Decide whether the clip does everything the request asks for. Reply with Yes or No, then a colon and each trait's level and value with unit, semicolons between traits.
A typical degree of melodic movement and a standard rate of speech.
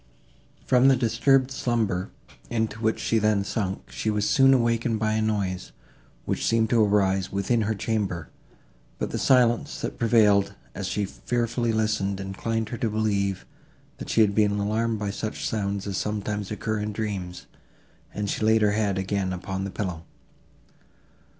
No: narrow, 2.3 semitones; average, 165 wpm